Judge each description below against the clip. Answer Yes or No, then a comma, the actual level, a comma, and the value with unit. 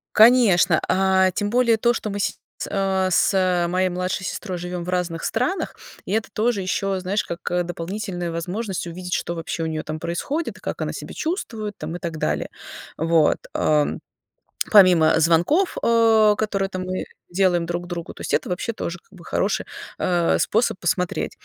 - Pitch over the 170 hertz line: Yes, medium, 185 Hz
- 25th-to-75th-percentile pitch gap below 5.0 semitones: Yes, average, 3.3 semitones